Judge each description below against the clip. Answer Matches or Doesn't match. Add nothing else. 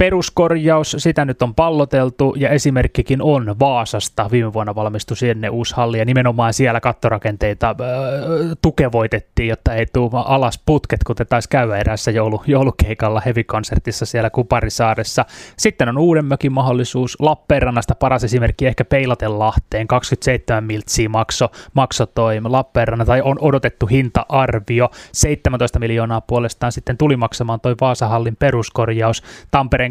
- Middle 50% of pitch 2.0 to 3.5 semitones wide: Matches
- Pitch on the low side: Matches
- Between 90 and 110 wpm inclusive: Doesn't match